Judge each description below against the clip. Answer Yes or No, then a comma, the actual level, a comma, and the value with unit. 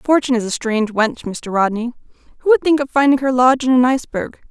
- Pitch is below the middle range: No, very high, 250 Hz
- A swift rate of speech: Yes, fast, 225 wpm